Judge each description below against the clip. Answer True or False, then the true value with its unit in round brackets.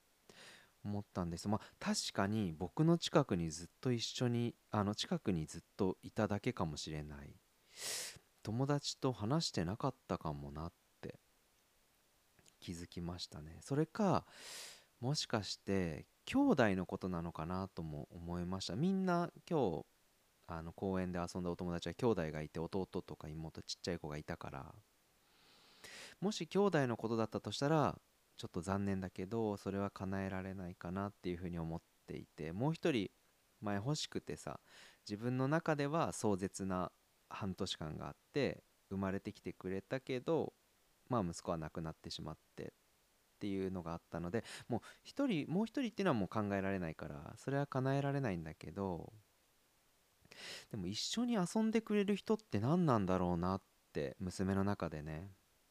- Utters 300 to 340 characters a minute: True (325 characters per minute)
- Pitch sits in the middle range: False (95 Hz)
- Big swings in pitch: True (7.0 semitones)